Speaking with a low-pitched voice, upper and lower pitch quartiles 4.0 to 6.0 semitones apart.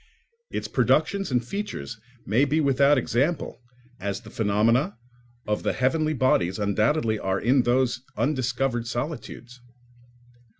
Yes: low, 125 Hz; average, 4.3 semitones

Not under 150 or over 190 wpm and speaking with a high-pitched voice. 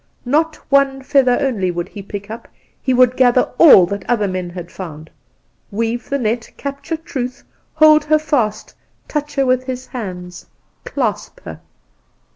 Yes: average, 155 wpm; high, 245 Hz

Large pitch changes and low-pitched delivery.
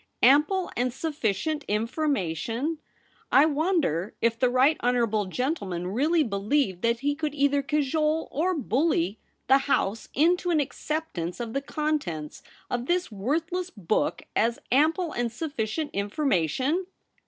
No: wide, 5.9 semitones; very high, 275 Hz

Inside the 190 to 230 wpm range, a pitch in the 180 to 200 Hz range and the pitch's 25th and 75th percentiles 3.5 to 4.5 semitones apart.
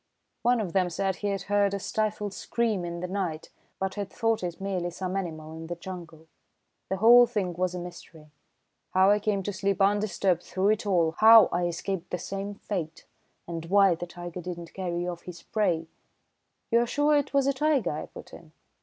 No: fast, 205 wpm; high, 190 Hz; average, 3.1 semitones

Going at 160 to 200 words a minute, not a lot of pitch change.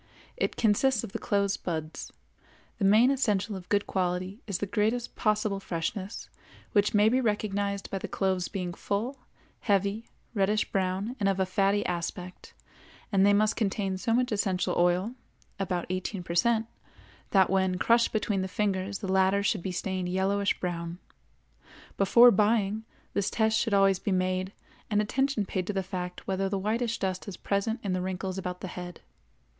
Yes: average, 170 wpm; narrow, 2.2 semitones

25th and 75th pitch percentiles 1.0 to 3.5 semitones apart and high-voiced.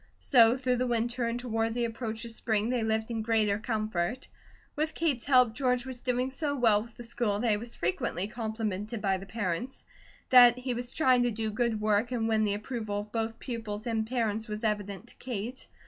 Yes: narrow, 2.4 semitones; high, 225 Hz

